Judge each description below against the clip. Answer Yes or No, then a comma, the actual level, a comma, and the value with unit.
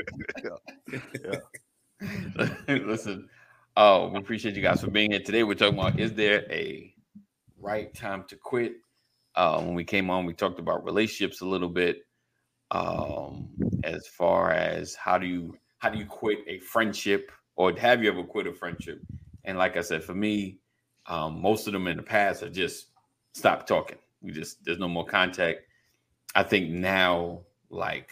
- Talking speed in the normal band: Yes, average, 175 wpm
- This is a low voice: Yes, very low, 95 Hz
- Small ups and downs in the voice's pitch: No, average, 3.0 semitones